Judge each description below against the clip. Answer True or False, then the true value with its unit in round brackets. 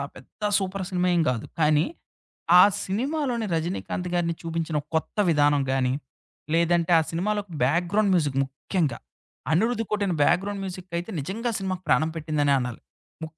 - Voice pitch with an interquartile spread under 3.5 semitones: False (4.3 semitones)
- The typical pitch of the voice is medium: True (175 Hz)